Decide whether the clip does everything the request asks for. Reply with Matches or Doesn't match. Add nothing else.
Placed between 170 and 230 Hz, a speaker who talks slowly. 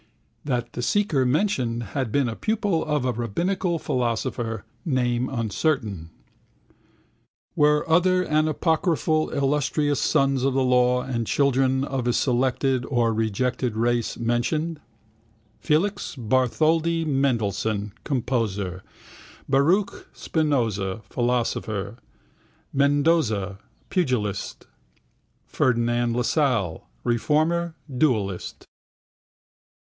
Doesn't match